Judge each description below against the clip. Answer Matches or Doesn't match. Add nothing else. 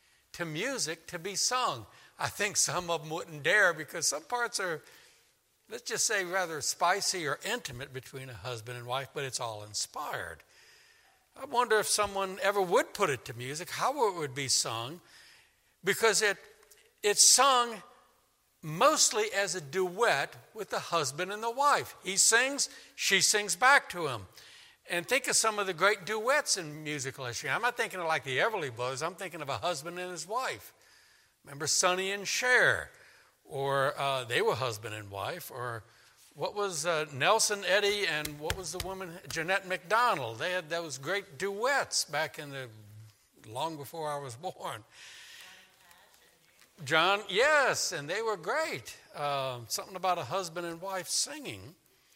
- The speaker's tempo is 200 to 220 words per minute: Doesn't match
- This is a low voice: Doesn't match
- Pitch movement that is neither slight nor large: Doesn't match